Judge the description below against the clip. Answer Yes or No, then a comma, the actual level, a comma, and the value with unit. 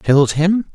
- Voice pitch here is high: No, medium, 160 Hz